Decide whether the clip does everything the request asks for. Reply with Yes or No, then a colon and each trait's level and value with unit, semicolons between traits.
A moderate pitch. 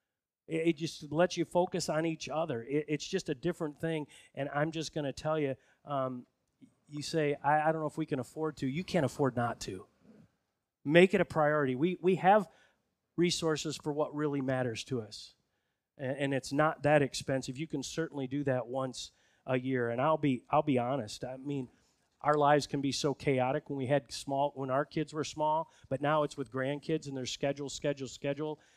Yes: medium, 145 Hz